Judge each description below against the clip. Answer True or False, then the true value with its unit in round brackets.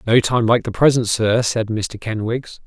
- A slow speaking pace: False (200 wpm)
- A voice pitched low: True (115 Hz)